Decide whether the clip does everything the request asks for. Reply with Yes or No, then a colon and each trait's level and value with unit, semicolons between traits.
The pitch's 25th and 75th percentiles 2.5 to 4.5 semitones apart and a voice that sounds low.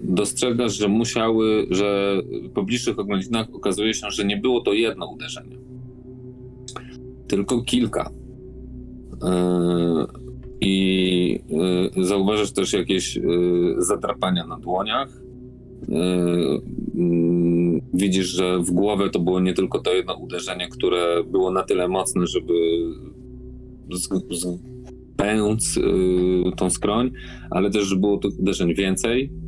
No: wide, 5.5 semitones; very low, 95 Hz